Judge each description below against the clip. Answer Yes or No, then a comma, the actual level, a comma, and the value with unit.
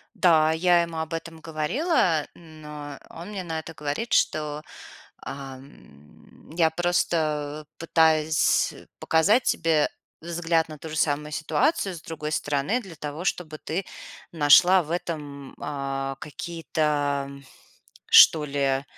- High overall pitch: No, medium, 155 Hz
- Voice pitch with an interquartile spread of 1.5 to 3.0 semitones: Yes, narrow, 2.4 semitones